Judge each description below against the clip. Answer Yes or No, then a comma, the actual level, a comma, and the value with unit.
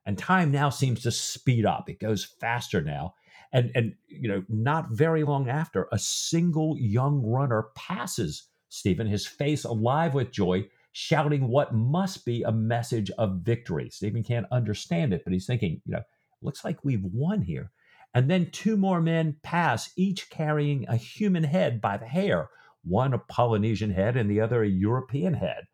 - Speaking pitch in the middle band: No, low, 125 Hz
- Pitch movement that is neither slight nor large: No, wide, 6.0 semitones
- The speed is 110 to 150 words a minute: No, average, 175 wpm